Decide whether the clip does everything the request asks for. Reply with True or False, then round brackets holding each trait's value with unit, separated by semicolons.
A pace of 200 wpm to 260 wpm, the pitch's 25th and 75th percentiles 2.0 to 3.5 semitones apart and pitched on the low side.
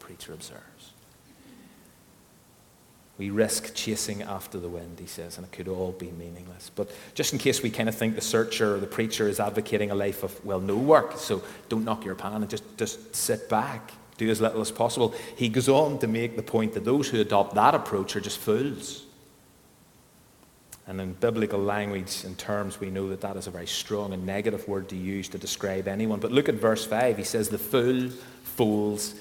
True (205 wpm; 2.7 semitones; 105 Hz)